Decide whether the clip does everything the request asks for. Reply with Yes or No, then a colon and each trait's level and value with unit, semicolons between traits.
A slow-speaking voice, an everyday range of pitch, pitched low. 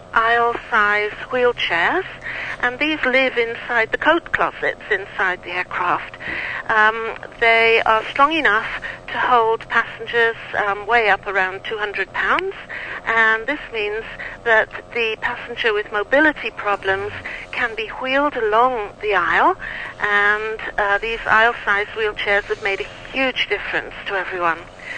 No: slow, 130 wpm; average, 3.5 semitones; high, 230 Hz